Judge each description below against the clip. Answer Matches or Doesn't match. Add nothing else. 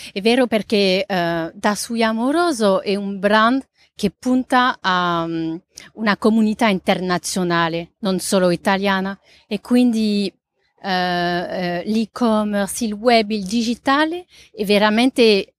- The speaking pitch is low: Doesn't match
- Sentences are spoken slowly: Matches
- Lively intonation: Doesn't match